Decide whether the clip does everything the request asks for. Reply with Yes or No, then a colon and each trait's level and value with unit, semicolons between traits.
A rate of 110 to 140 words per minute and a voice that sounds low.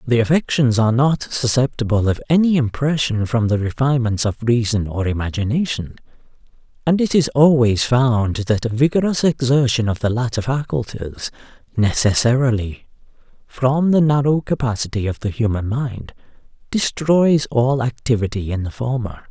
Yes: slow, 135 wpm; low, 120 Hz